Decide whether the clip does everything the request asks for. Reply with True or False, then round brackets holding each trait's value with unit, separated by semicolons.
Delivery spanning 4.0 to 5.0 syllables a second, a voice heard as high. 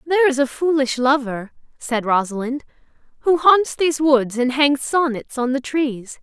True (4.6 syllables/s; 270 Hz)